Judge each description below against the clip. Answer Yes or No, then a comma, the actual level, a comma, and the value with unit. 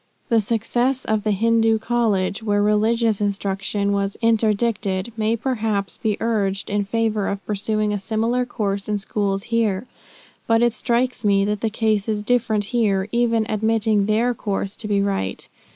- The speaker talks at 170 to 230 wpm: No, average, 160 wpm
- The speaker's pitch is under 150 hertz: No, high, 215 Hz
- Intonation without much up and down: Yes, narrow, 2.3 semitones